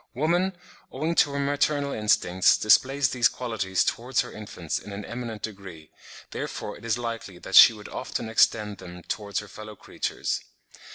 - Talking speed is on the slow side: No, average, 165 wpm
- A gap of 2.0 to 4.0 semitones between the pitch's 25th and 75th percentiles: No, average, 4.7 semitones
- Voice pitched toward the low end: Yes, low, 110 Hz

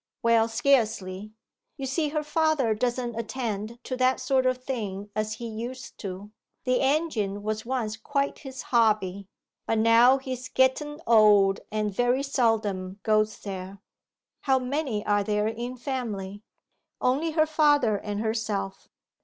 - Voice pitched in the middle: No, high, 230 Hz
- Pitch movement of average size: Yes, average, 3.9 semitones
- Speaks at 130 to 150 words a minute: Yes, average, 140 wpm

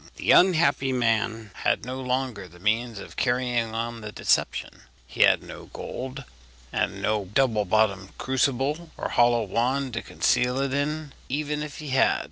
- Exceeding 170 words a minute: No, average, 160 wpm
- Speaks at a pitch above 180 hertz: No, low, 125 Hz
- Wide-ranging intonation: No, average, 3.5 semitones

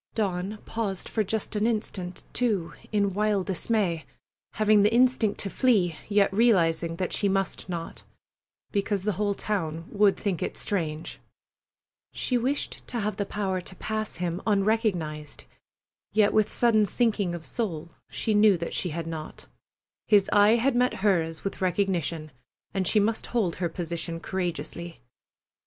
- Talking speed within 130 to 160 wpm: Yes, average, 150 wpm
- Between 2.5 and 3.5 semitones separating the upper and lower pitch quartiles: No, average, 3.9 semitones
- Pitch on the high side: Yes, high, 200 Hz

